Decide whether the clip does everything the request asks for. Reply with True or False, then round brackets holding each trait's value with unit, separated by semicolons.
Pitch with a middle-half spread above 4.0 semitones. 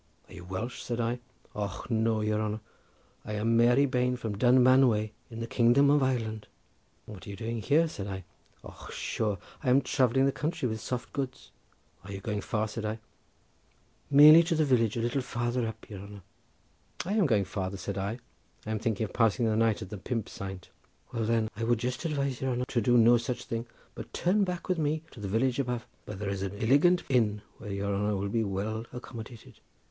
False (3.4 semitones)